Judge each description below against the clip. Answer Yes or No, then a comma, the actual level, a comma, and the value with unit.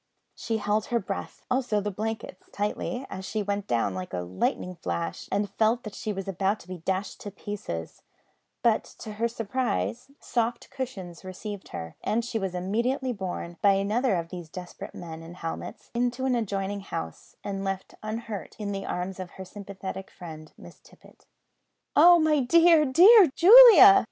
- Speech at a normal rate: Yes, average, 170 wpm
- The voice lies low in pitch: No, high, 200 Hz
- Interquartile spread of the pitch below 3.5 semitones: No, average, 4.4 semitones